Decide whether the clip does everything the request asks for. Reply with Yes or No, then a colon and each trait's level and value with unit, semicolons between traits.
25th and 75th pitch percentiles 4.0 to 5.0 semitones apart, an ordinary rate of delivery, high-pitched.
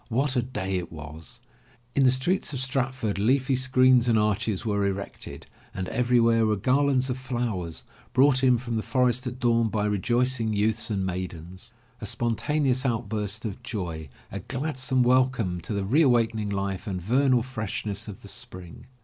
No: average, 4.3 semitones; average, 170 wpm; low, 115 Hz